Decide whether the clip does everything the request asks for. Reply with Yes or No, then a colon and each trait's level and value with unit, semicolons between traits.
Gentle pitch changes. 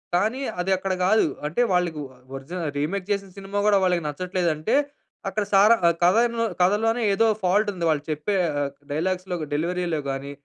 No: average, 3.3 semitones